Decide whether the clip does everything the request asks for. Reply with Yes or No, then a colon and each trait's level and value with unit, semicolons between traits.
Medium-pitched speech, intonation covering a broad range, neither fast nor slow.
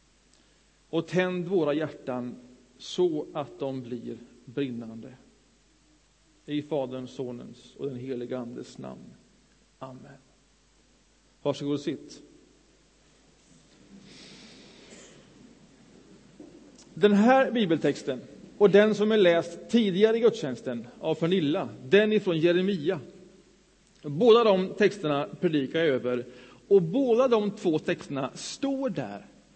No: medium, 165 Hz; wide, 7.2 semitones; slow, 100 wpm